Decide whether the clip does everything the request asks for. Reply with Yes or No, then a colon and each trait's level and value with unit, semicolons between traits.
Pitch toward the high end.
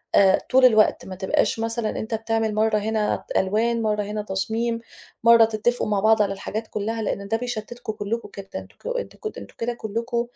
Yes: high, 220 Hz